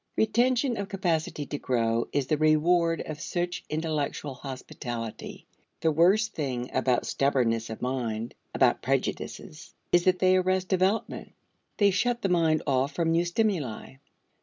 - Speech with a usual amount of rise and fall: No, wide, 5.9 semitones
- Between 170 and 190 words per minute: No, average, 140 wpm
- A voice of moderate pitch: Yes, medium, 160 Hz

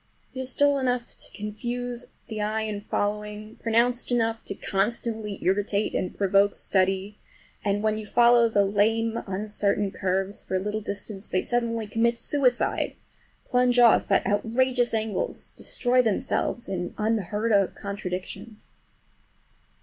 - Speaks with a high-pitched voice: Yes, high, 215 Hz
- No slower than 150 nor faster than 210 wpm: No, slow, 135 wpm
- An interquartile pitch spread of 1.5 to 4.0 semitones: Yes, average, 2.8 semitones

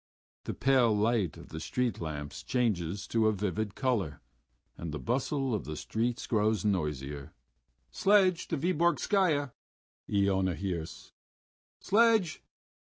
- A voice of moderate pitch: No, low, 110 Hz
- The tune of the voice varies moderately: No, wide, 7.5 semitones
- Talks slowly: Yes, slow, 120 wpm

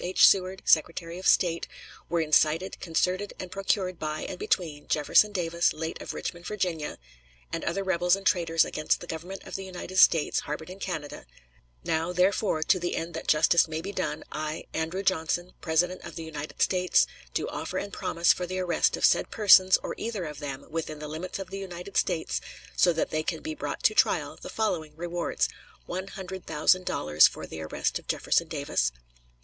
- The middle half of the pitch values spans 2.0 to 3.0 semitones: Yes, average, 2.7 semitones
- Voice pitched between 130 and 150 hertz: No, medium, 175 Hz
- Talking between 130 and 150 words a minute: No, average, 190 wpm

